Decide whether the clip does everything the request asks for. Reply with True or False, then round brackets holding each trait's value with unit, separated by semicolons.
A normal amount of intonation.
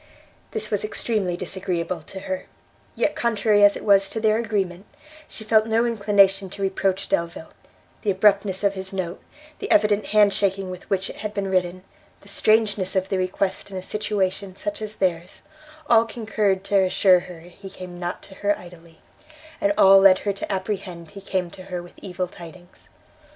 False (2.1 semitones)